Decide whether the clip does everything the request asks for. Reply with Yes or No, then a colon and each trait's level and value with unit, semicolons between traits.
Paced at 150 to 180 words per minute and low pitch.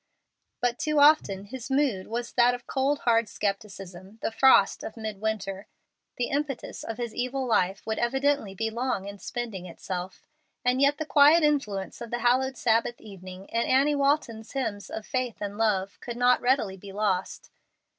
No: average, 170 wpm; high, 230 Hz